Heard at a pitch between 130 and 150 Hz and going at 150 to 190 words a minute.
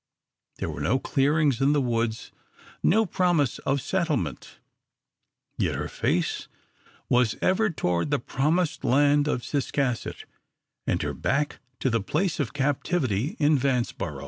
No: medium, 140 Hz; slow, 135 wpm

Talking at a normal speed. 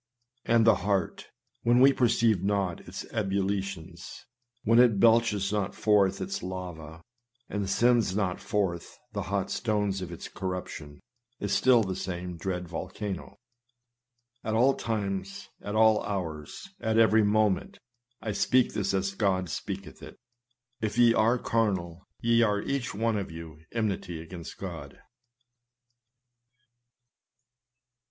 No: slow, 130 wpm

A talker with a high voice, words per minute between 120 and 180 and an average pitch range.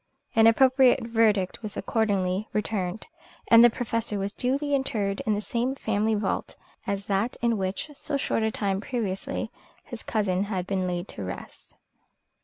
Yes: high, 215 Hz; average, 160 wpm; average, 3.0 semitones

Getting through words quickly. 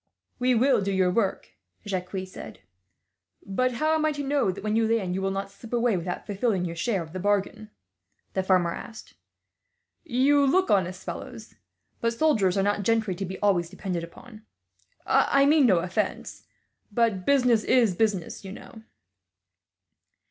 No: average, 165 wpm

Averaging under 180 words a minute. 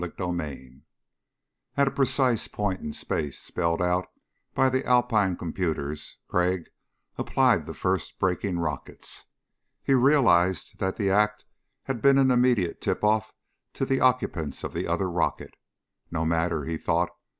Yes: average, 145 wpm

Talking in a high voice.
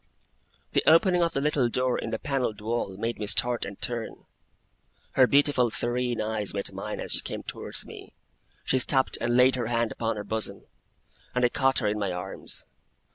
No: low, 120 Hz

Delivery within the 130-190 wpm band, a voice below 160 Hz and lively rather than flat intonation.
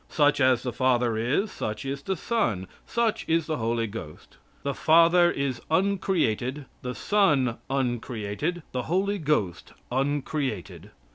Yes: slow, 135 wpm; low, 135 Hz; wide, 6.0 semitones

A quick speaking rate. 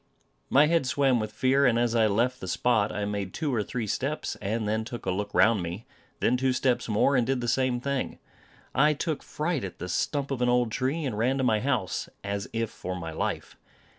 Yes: fast, 225 wpm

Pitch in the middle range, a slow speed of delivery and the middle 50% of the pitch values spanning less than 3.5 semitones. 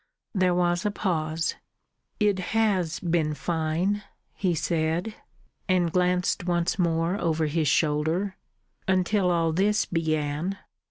Yes: medium, 175 Hz; slow, 115 wpm; narrow, 2.6 semitones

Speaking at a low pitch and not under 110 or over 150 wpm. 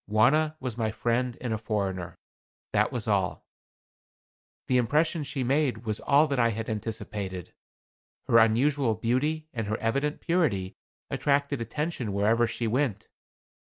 Yes: low, 120 Hz; average, 140 wpm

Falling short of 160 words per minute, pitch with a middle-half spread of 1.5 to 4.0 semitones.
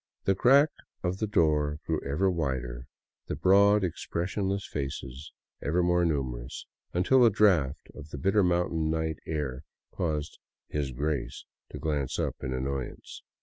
No: average, 150 wpm; average, 5.2 semitones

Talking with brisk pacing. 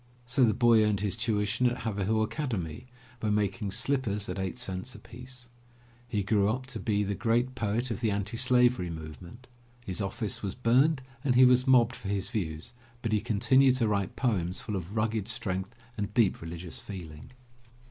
No: average, 180 wpm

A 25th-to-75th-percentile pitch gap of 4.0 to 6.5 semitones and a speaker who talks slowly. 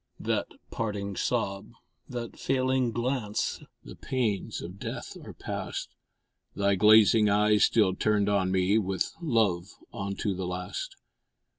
No: average, 2.8 semitones; slow, 125 wpm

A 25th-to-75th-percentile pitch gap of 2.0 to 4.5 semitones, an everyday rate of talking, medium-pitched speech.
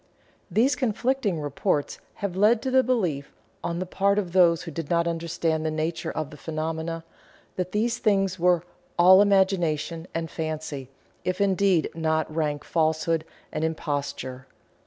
Yes: average, 3.6 semitones; average, 150 wpm; medium, 170 Hz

